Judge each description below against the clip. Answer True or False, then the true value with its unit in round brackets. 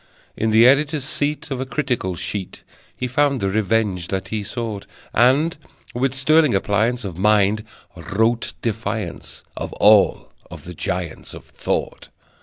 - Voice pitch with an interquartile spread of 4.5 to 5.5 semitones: True (4.8 semitones)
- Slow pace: False (145 wpm)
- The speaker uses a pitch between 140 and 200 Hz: False (110 Hz)